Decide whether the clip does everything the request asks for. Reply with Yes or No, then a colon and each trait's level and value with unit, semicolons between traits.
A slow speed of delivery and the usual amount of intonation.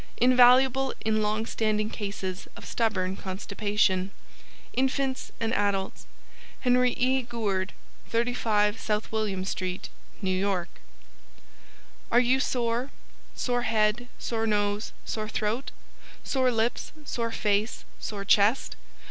Yes: slow, 110 wpm; average, 3.2 semitones